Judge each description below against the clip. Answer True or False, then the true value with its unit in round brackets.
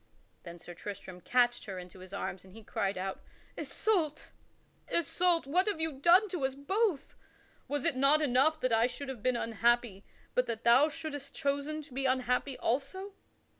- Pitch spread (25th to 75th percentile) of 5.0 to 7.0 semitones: True (5.3 semitones)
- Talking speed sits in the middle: True (180 wpm)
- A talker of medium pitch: False (265 Hz)